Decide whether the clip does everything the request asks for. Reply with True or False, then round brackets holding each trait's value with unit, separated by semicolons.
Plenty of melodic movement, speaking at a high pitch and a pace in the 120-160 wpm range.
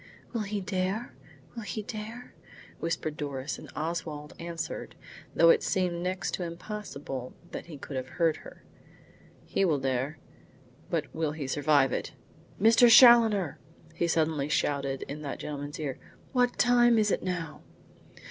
False (6.0 semitones; 165 Hz; 145 wpm)